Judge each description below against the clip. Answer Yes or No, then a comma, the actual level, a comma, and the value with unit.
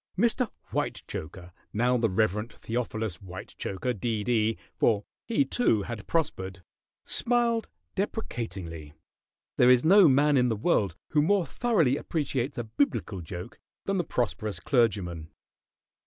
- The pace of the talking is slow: Yes, slow, 125 wpm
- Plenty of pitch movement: Yes, wide, 7.3 semitones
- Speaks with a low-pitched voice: Yes, low, 120 Hz